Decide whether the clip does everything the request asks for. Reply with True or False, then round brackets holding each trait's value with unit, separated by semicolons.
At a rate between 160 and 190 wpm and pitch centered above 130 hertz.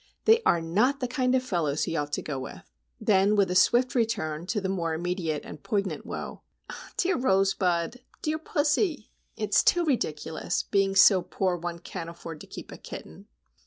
True (170 wpm; 190 Hz)